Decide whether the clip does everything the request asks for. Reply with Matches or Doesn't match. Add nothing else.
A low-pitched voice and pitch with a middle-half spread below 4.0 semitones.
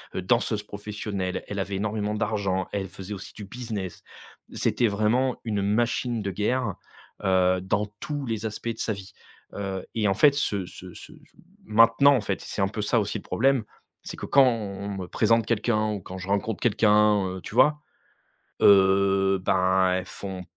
Matches